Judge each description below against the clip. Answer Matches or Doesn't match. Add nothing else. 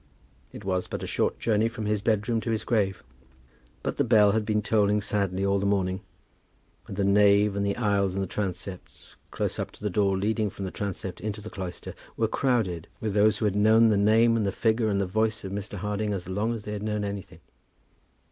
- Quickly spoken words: Matches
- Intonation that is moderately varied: Doesn't match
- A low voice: Matches